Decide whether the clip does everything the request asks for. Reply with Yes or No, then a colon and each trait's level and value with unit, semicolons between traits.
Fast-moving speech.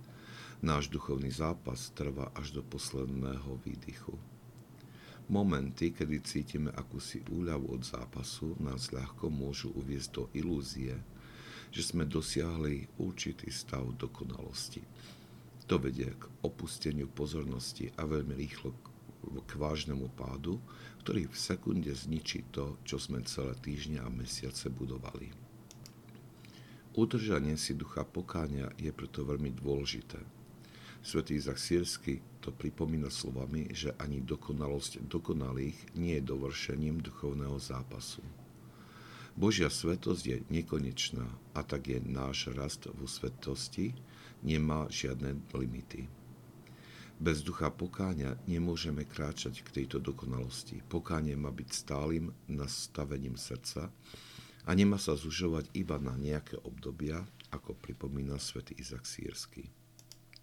No: average, 115 wpm